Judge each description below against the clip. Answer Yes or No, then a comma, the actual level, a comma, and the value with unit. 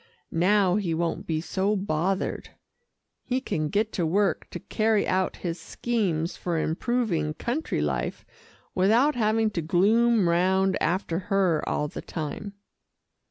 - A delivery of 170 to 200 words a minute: No, slow, 135 wpm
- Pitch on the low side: No, high, 190 Hz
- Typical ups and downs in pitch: Yes, average, 4.2 semitones